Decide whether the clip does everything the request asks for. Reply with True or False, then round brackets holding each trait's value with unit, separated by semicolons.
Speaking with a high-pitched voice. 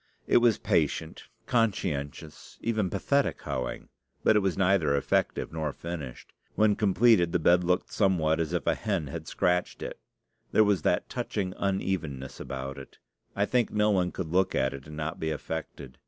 False (90 Hz)